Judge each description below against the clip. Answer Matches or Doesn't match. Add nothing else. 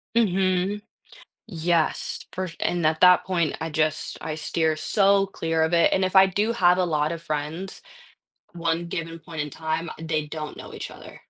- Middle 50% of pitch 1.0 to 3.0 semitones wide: Matches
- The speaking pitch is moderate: Matches